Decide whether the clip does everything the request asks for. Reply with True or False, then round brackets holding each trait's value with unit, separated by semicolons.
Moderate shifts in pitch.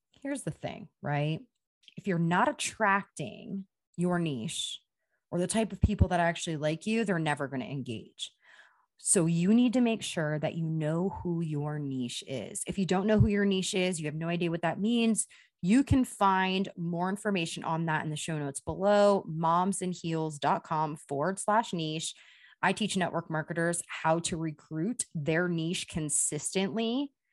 True (3.8 semitones)